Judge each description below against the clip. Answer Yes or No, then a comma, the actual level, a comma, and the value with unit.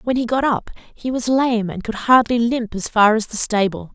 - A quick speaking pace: Yes, fast, 245 wpm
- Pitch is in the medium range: No, high, 230 Hz